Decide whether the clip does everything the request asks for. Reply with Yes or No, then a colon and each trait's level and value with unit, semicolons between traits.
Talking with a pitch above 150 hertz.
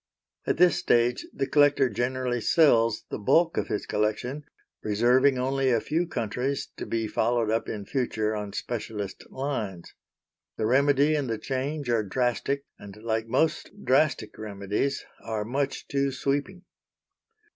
No: low, 125 Hz